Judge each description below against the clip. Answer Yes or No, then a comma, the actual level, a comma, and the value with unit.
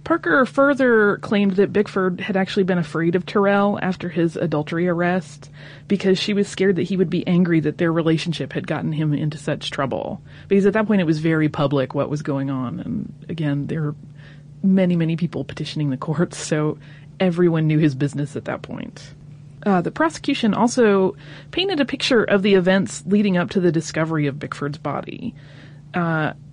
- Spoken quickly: No, average, 185 wpm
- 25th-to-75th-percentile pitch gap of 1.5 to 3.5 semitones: No, average, 4.7 semitones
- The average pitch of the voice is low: No, medium, 170 Hz